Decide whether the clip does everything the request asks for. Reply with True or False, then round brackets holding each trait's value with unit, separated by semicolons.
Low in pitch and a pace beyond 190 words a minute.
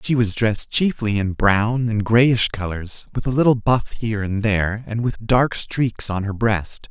True (110 Hz; 200 wpm)